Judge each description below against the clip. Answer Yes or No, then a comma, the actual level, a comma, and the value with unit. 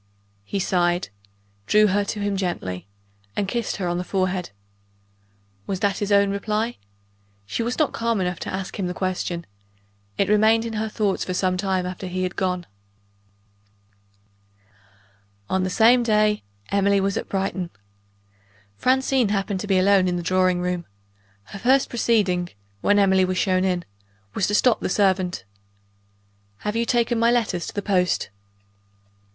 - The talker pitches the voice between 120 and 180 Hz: No, high, 195 Hz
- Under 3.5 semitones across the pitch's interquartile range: Yes, narrow, 2.6 semitones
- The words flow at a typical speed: Yes, average, 160 wpm